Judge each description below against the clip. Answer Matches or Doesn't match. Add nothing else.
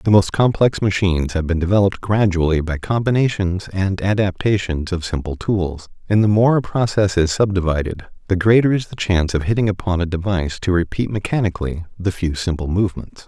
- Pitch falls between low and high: Doesn't match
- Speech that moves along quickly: Doesn't match